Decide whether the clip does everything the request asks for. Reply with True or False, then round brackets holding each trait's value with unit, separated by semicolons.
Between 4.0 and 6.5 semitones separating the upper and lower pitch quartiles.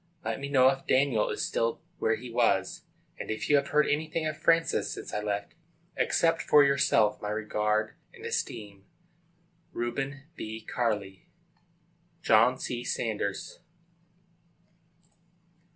True (4.8 semitones)